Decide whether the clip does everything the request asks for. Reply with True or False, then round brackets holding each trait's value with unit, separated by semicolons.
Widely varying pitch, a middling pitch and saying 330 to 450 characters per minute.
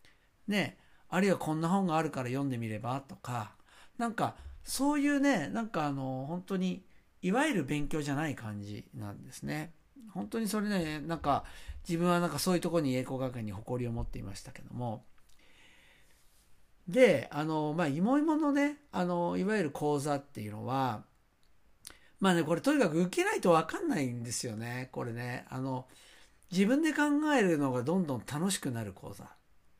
True (7.5 semitones; 150 Hz; 340 characters per minute)